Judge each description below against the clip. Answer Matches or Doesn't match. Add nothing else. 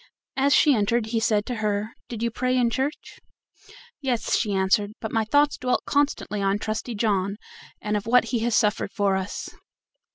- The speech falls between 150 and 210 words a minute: Matches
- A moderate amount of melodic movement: Matches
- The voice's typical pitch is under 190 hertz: Doesn't match